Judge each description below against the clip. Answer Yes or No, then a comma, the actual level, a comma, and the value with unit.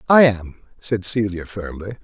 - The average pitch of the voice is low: Yes, low, 105 Hz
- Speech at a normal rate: Yes, average, 150 wpm